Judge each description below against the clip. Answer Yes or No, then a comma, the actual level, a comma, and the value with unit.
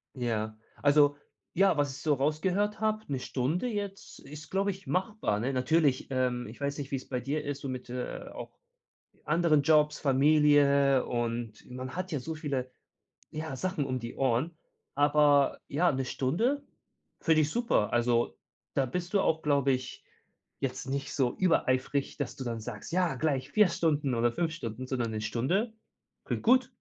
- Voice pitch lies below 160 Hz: Yes, medium, 140 Hz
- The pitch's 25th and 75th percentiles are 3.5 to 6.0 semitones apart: Yes, average, 4.1 semitones